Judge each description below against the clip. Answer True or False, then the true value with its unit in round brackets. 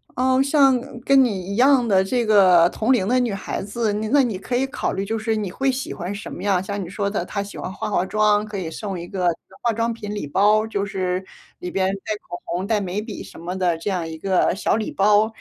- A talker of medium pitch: False (205 Hz)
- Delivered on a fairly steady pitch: False (3.2 semitones)